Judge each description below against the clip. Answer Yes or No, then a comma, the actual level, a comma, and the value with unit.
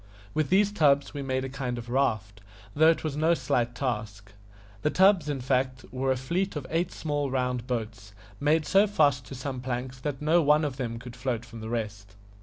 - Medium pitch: No, low, 130 Hz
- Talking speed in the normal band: No, fast, 210 wpm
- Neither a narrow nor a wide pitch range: Yes, average, 3.6 semitones